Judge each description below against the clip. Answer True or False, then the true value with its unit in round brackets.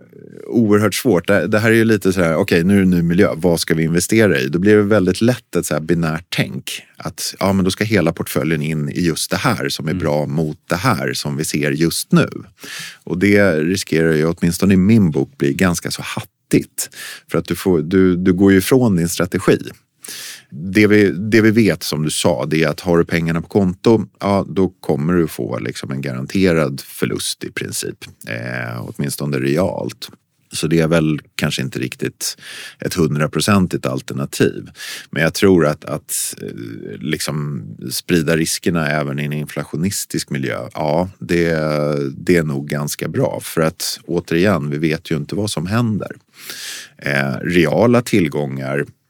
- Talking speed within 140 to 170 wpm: False (185 wpm)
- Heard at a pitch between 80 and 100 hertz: True (85 Hz)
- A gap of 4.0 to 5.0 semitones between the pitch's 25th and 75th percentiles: True (4.3 semitones)